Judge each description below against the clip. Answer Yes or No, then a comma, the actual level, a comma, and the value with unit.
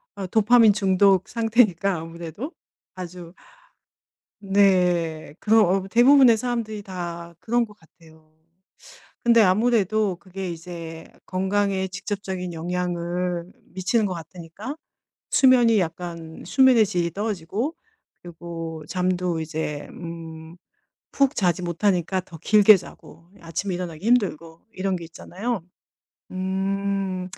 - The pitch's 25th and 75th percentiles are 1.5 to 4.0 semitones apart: Yes, average, 3.5 semitones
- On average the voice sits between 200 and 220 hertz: No, medium, 185 Hz